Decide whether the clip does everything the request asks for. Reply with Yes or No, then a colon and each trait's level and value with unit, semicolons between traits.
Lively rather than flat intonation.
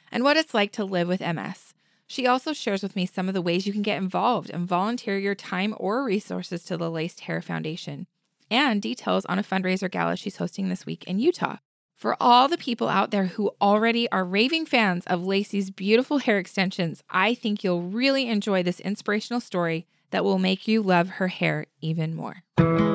No: average, 3.4 semitones